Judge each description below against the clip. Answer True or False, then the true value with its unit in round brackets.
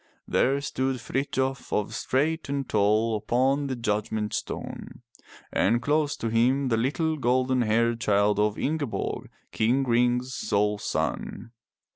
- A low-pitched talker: True (120 Hz)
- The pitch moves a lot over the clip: False (3.6 semitones)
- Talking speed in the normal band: False (125 wpm)